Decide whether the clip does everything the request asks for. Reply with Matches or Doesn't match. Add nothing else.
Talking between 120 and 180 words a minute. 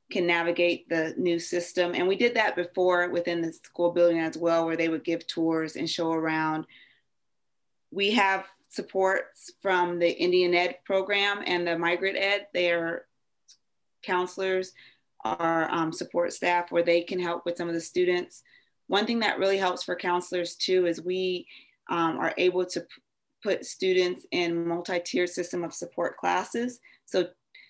Matches